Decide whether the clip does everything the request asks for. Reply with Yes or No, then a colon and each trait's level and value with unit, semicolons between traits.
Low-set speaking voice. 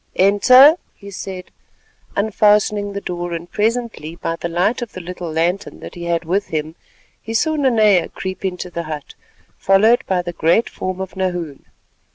No: medium, 185 Hz